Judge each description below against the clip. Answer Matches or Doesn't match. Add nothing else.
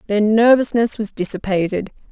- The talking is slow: Matches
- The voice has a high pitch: Matches